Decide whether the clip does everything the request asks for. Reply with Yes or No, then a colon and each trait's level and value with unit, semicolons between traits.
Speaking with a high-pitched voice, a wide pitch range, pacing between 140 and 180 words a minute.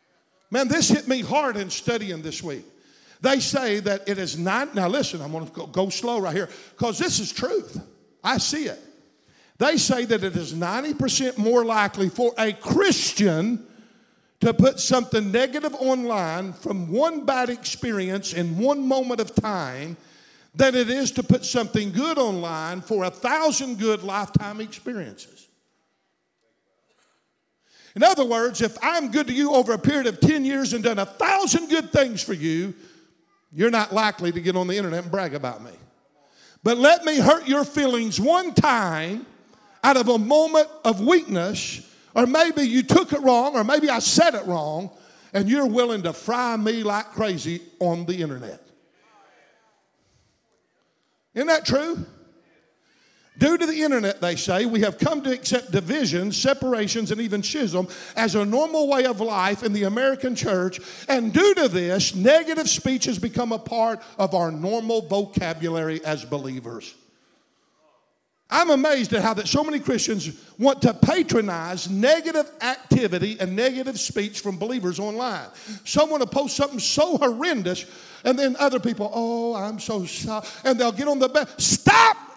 Yes: high, 230 Hz; wide, 5.7 semitones; average, 165 wpm